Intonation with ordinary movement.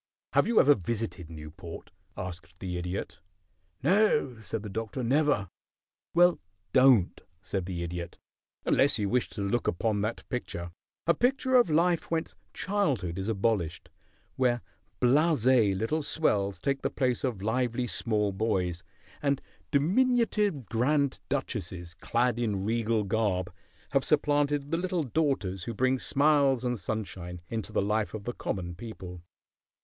No: wide, 6.6 semitones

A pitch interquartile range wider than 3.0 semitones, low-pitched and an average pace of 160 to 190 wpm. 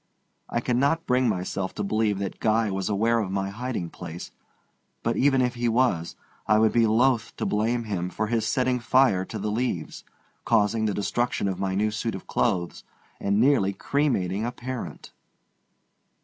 Yes: average, 3.8 semitones; low, 110 Hz; average, 175 wpm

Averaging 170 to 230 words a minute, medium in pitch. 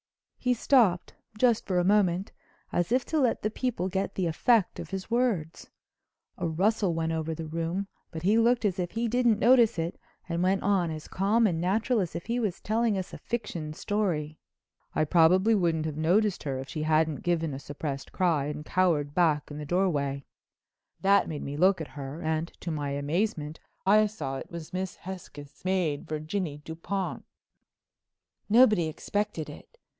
Yes: average, 175 wpm; medium, 175 Hz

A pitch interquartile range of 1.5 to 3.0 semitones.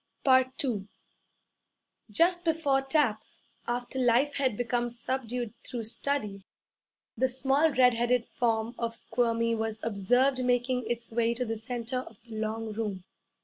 Yes: narrow, 2.5 semitones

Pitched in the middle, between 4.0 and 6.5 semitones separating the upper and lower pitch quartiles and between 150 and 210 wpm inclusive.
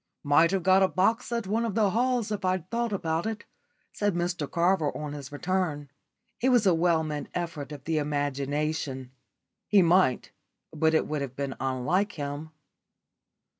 Yes: medium, 165 Hz; average, 4.9 semitones; average, 170 wpm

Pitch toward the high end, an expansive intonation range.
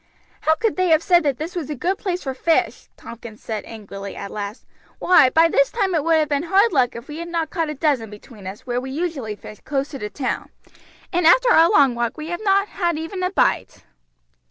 Yes: very high, 305 Hz; wide, 6.2 semitones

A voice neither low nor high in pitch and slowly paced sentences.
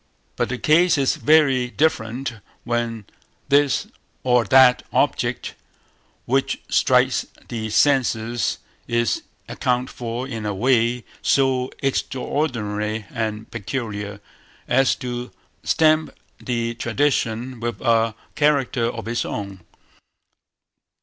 No: low, 120 Hz; slow, 105 wpm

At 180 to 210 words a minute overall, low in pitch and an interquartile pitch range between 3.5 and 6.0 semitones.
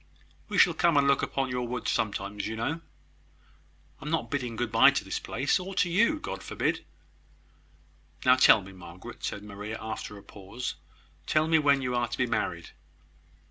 Yes: average, 185 wpm; low, 125 Hz; average, 5.3 semitones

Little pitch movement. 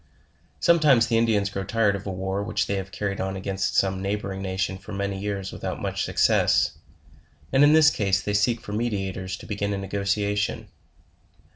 Yes: narrow, 1.5 semitones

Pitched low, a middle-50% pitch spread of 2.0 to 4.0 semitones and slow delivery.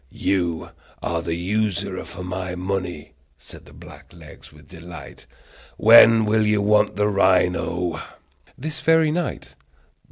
Yes: very low, 95 Hz; average, 3.4 semitones; slow, 125 wpm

